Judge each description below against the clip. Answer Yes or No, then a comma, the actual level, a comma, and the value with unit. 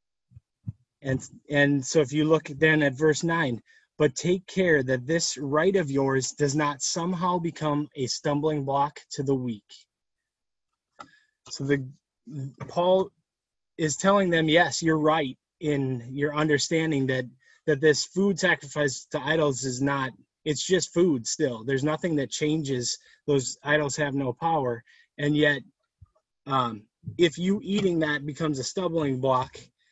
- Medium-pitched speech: Yes, medium, 150 Hz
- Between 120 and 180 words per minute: Yes, average, 145 wpm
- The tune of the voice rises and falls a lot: No, average, 3.1 semitones